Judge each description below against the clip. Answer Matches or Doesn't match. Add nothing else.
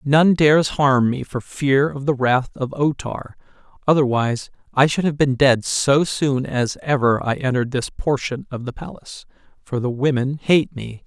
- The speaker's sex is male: Matches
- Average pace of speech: Matches